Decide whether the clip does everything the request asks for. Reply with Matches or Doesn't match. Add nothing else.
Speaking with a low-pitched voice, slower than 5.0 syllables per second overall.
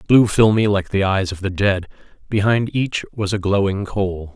Matches